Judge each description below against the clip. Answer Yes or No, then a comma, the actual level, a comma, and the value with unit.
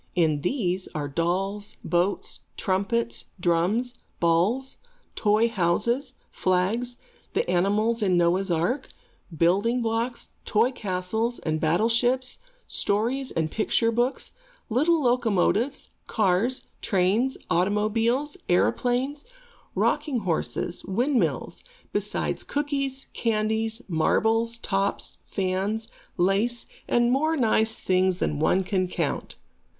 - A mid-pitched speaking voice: No, high, 215 Hz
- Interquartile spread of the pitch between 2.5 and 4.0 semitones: No, average, 4.9 semitones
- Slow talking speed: Yes, slow, 100 wpm